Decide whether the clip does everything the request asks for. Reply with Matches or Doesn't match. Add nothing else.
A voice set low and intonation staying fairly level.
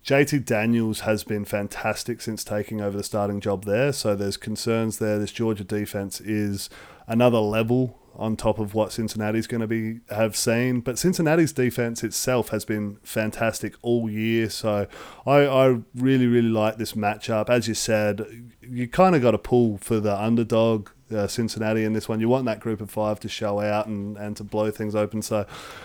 Matches